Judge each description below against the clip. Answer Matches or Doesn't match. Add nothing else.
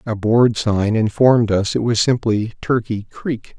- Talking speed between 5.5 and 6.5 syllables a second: Doesn't match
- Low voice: Matches